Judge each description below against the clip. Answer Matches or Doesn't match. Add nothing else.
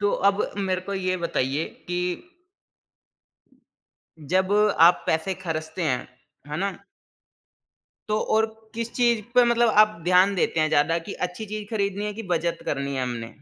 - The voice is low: Doesn't match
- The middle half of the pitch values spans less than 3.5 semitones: Doesn't match